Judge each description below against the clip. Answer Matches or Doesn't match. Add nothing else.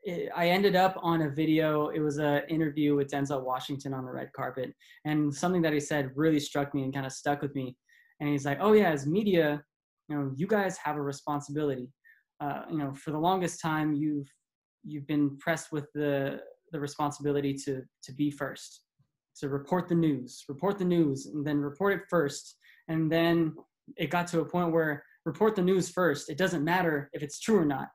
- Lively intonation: Doesn't match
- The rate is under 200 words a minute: Doesn't match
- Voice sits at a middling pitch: Matches